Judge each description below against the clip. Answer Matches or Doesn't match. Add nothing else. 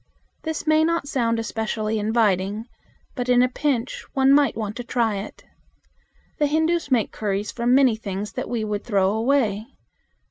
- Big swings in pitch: Doesn't match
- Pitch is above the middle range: Matches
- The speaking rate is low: Doesn't match